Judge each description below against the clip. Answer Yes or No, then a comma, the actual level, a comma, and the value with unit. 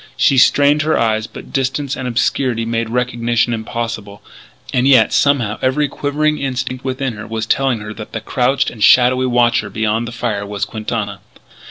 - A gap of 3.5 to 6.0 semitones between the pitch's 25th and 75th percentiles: No, average, 3.0 semitones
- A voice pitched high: No, low, 120 Hz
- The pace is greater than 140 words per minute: Yes, average, 170 wpm